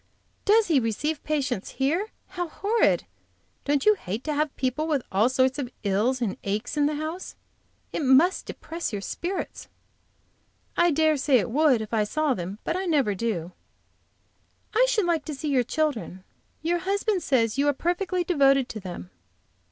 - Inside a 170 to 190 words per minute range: Yes, average, 175 wpm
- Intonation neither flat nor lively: No, wide, 6.1 semitones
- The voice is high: Yes, very high, 290 Hz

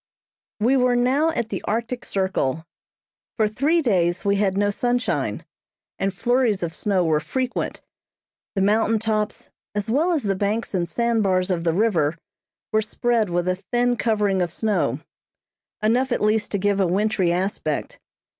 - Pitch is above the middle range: Yes, high, 210 Hz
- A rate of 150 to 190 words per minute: Yes, average, 165 wpm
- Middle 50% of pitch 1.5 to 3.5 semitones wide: No, average, 4.1 semitones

